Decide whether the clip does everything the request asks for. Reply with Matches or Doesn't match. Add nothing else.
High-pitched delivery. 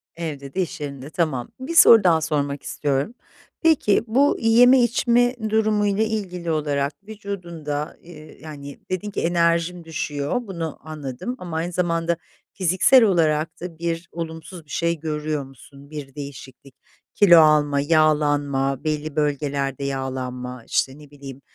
Doesn't match